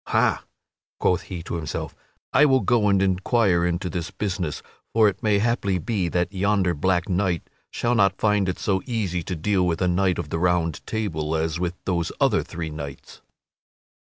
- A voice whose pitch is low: Yes, very low, 90 Hz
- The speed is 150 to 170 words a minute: No, average, 190 wpm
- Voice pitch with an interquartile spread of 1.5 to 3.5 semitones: Yes, average, 3.1 semitones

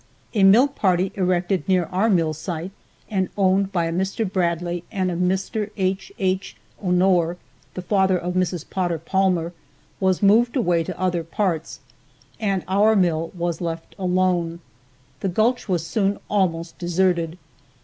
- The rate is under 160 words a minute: Yes, average, 150 wpm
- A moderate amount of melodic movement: No, narrow, 2.1 semitones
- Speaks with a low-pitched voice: No, medium, 185 Hz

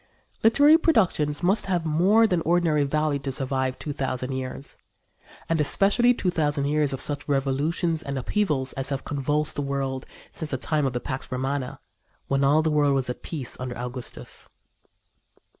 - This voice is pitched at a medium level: Yes, medium, 145 Hz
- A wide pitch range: No, average, 3.4 semitones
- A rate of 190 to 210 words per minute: No, average, 170 wpm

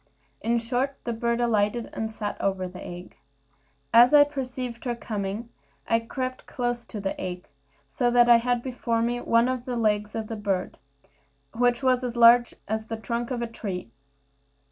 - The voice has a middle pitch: No, high, 235 Hz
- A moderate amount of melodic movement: No, narrow, 2.2 semitones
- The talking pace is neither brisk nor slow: Yes, average, 180 wpm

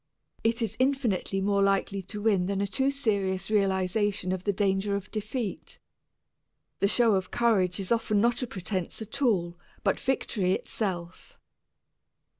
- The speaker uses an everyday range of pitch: Yes, average, 3.0 semitones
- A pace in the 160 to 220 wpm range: No, average, 150 wpm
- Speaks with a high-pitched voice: Yes, high, 200 Hz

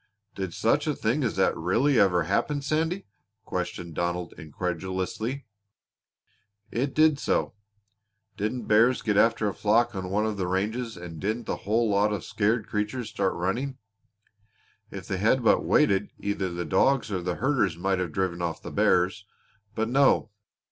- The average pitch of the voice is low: Yes, low, 105 Hz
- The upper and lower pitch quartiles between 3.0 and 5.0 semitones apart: Yes, average, 4.5 semitones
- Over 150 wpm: Yes, average, 160 wpm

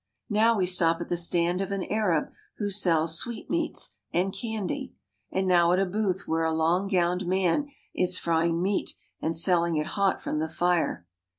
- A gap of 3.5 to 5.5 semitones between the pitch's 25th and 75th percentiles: No, average, 2.8 semitones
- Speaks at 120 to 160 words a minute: No, average, 185 wpm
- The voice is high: No, medium, 180 Hz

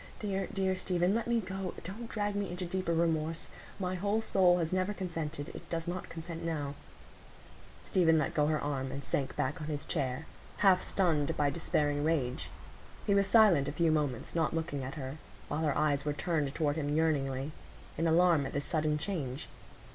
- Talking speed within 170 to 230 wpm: Yes, average, 185 wpm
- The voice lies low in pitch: No, medium, 160 Hz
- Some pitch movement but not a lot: Yes, average, 4.0 semitones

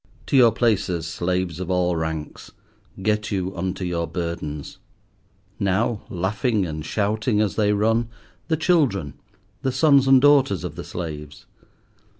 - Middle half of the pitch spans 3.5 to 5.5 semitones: Yes, average, 5.2 semitones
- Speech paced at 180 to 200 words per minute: No, average, 140 wpm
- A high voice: No, low, 100 Hz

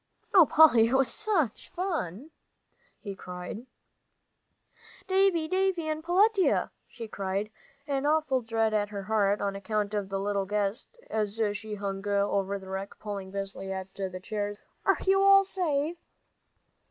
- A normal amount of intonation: No, wide, 8.0 semitones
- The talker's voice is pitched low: No, high, 215 Hz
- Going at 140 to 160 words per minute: Yes, average, 145 wpm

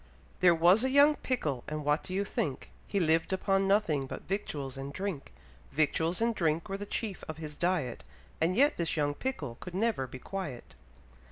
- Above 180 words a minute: Yes, average, 190 wpm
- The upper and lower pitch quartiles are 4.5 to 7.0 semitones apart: Yes, average, 5.1 semitones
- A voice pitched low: No, medium, 170 Hz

